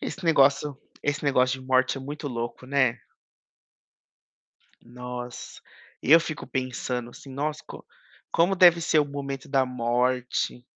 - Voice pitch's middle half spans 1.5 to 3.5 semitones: Yes, average, 2.7 semitones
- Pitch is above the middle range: No, low, 135 Hz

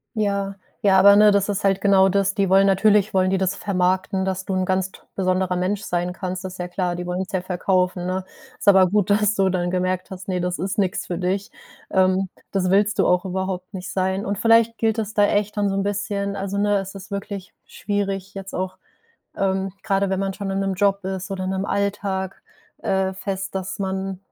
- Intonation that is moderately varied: No, narrow, 1.2 semitones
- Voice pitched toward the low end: No, high, 190 Hz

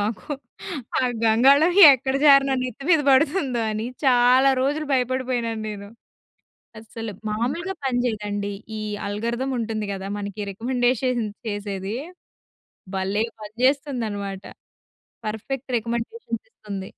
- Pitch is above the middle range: Yes, high, 235 Hz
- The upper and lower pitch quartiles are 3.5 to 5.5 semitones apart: Yes, average, 4.0 semitones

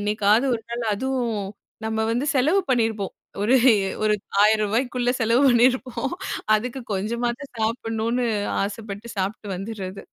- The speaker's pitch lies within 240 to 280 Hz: No, high, 225 Hz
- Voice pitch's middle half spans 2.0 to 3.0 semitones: Yes, average, 2.7 semitones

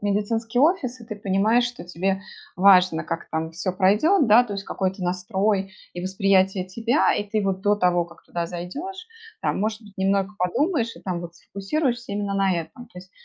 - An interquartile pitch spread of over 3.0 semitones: Yes, average, 3.6 semitones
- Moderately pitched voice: No, high, 195 Hz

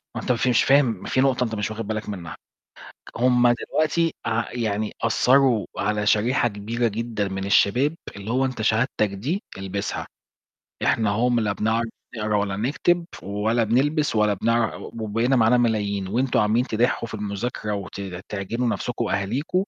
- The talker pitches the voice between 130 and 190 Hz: No, low, 115 Hz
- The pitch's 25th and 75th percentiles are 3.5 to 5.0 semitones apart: No, average, 3.0 semitones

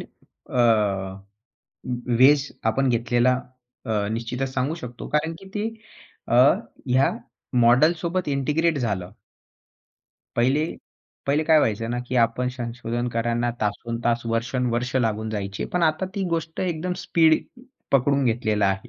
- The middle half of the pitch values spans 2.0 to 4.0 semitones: No, average, 4.5 semitones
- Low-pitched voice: Yes, low, 125 Hz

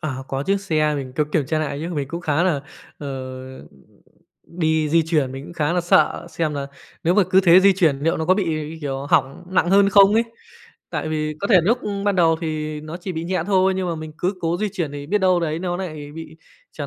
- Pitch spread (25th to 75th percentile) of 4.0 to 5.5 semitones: No, average, 3.2 semitones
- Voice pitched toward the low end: No, medium, 165 Hz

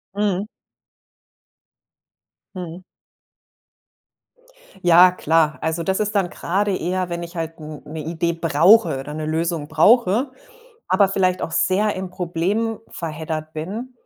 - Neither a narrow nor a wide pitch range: Yes, average, 3.2 semitones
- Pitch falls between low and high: Yes, medium, 175 Hz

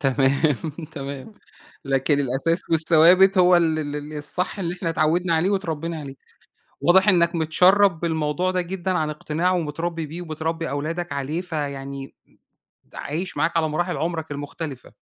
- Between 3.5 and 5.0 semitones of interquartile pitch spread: No, average, 3.1 semitones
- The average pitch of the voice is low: No, medium, 160 Hz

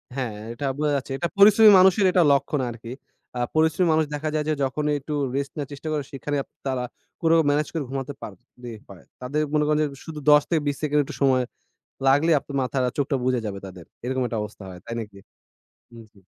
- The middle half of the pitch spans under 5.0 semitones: Yes, average, 3.4 semitones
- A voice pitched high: No, medium, 140 Hz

